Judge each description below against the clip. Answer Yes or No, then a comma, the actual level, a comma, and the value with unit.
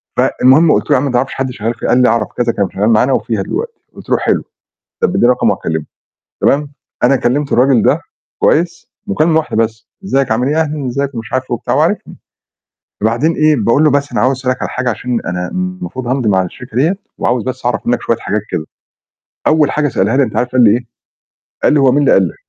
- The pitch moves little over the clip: No, average, 3.8 semitones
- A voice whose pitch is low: Yes, low, 125 Hz